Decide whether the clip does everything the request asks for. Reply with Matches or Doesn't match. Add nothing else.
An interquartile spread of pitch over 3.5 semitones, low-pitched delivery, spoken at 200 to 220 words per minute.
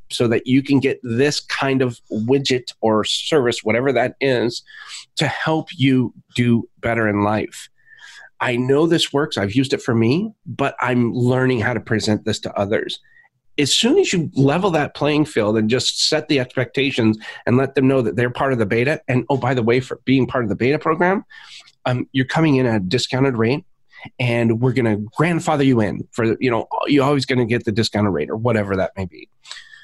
Matches